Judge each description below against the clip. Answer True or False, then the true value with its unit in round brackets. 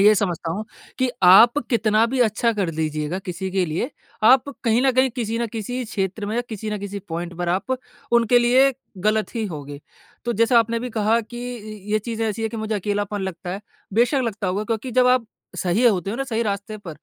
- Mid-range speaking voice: False (215 Hz)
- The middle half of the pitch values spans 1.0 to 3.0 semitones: False (3.5 semitones)